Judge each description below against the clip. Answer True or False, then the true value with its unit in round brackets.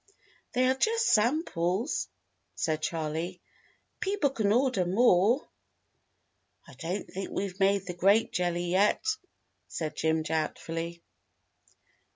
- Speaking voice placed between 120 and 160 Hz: False (185 Hz)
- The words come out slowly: True (110 wpm)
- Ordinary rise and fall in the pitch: False (5.8 semitones)